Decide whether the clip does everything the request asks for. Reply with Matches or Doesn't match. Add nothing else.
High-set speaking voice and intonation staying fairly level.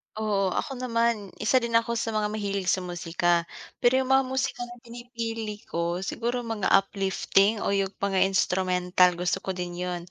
Doesn't match